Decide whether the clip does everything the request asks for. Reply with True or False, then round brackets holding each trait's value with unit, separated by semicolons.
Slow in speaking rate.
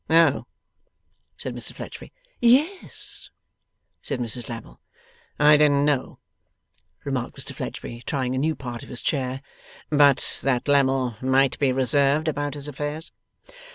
True (130 wpm)